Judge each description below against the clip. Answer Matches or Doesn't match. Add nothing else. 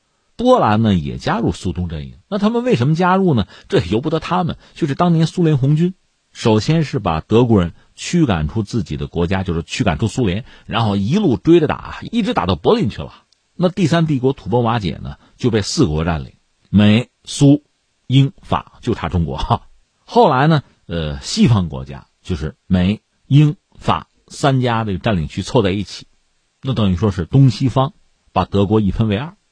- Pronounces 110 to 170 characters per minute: Doesn't match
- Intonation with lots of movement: Matches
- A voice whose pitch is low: Matches